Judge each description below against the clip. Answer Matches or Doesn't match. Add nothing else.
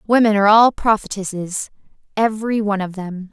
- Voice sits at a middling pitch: Doesn't match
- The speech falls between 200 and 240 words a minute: Doesn't match